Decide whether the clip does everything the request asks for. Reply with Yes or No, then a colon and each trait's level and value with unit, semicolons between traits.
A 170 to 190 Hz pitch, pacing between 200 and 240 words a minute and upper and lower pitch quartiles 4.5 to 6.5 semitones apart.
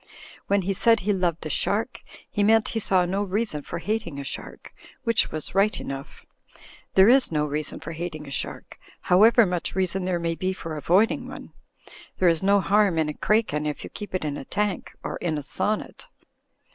Yes: medium, 185 Hz; fast, 205 wpm; average, 4.8 semitones